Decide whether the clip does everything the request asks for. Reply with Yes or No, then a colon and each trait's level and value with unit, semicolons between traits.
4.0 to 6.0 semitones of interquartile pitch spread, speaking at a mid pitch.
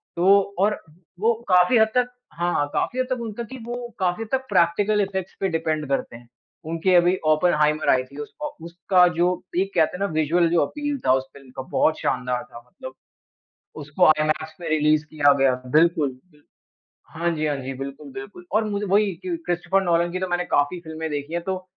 Yes: average, 4.4 semitones; medium, 170 Hz